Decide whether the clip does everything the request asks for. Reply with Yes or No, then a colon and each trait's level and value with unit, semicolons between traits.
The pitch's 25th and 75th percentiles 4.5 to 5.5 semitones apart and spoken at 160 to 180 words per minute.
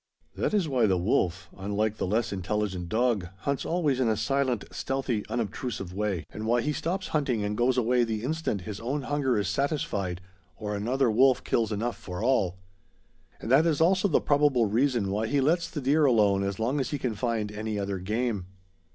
No: average, 4.8 semitones; average, 195 wpm